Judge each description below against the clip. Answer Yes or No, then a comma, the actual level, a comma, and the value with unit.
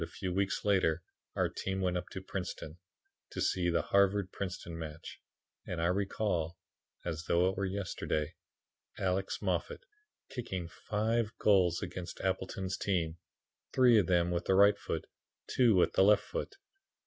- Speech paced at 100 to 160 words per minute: Yes, average, 155 wpm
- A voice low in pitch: Yes, very low, 95 Hz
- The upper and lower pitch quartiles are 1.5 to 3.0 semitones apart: Yes, narrow, 2.5 semitones